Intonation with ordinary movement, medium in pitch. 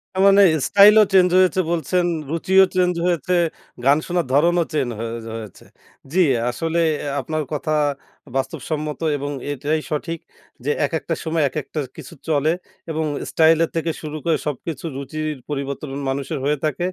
Yes: average, 3.1 semitones; medium, 155 Hz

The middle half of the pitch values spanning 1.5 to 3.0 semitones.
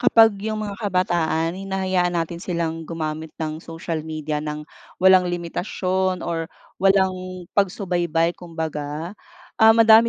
Yes: average, 2.7 semitones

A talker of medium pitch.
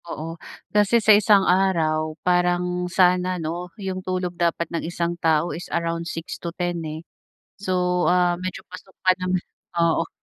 Yes: medium, 180 Hz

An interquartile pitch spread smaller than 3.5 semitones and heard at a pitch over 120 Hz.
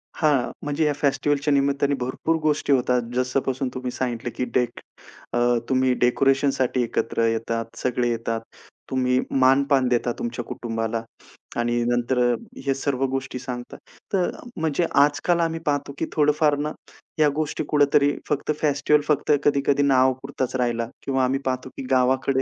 Yes: narrow, 2.6 semitones; low, 130 Hz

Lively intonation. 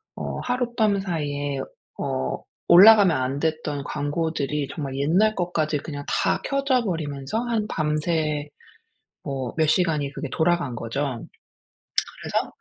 No: average, 4.5 semitones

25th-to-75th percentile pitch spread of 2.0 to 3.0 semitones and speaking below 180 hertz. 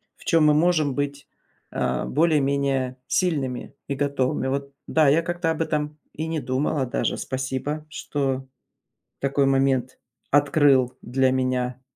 Yes: narrow, 2.5 semitones; medium, 140 Hz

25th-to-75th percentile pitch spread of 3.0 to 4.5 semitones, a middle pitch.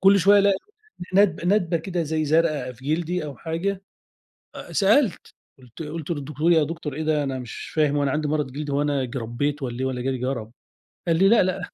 Yes: average, 4.2 semitones; medium, 155 Hz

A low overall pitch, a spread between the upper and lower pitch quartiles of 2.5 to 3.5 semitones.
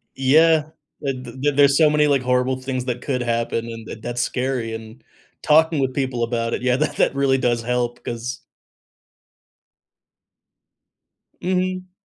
Yes: low, 130 Hz; average, 2.9 semitones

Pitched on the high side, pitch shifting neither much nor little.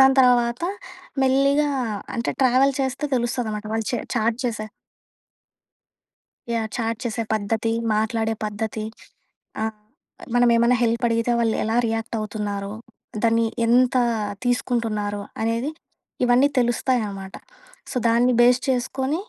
No: high, 235 Hz; narrow, 2.1 semitones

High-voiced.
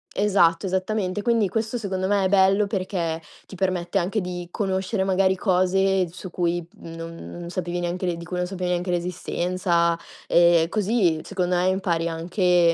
No: medium, 180 Hz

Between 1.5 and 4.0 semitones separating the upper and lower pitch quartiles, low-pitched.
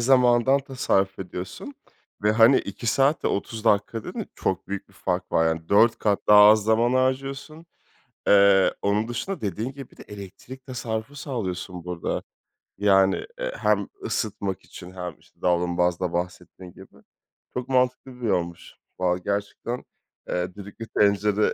No: average, 5.0 semitones; low, 105 Hz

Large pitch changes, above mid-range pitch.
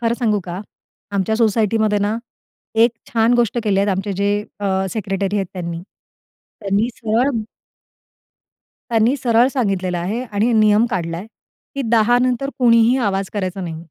No: average, 3.0 semitones; high, 210 Hz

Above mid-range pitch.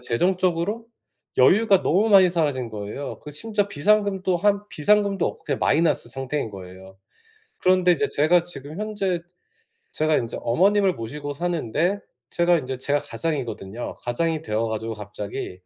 No: medium, 160 Hz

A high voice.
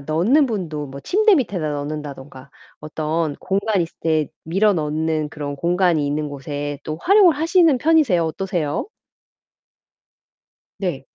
No: medium, 160 Hz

